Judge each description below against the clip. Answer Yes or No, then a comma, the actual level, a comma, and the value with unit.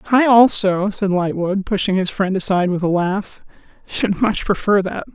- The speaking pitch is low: No, high, 195 Hz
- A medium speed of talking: Yes, average, 175 wpm